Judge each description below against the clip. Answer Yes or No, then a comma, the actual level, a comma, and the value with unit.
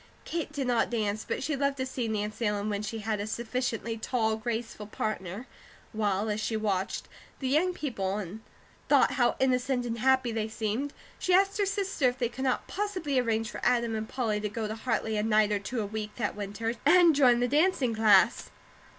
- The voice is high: Yes, high, 230 Hz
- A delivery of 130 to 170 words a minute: No, fast, 205 wpm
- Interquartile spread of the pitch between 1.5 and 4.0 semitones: Yes, average, 3.6 semitones